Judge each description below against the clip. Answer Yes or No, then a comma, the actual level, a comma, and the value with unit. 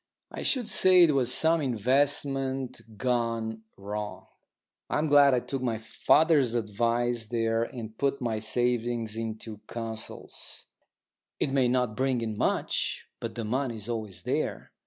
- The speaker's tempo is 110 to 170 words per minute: Yes, average, 140 wpm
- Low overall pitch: Yes, low, 120 Hz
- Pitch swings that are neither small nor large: Yes, average, 3.2 semitones